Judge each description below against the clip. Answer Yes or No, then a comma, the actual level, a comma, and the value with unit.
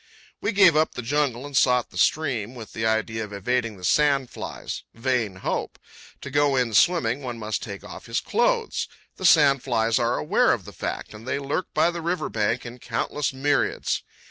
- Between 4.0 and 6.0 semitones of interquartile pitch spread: Yes, average, 4.5 semitones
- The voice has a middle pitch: No, low, 125 Hz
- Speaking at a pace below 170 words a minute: No, average, 195 wpm